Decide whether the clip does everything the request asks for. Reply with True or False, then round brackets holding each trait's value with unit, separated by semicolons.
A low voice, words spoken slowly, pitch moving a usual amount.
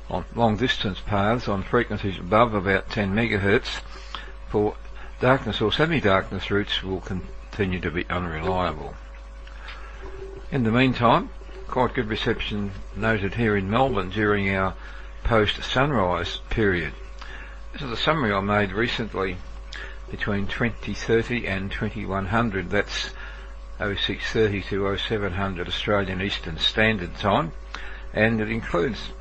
True (100 Hz; 115 wpm; 3.0 semitones)